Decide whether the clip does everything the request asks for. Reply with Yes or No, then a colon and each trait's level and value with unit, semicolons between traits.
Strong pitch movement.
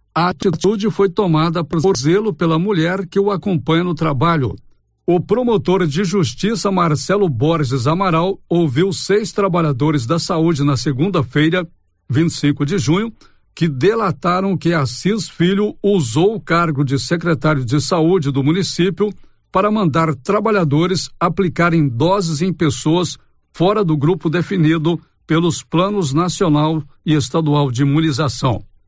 No: average, 3.8 semitones